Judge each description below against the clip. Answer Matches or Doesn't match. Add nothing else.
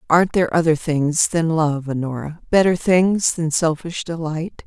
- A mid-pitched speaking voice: Matches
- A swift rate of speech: Doesn't match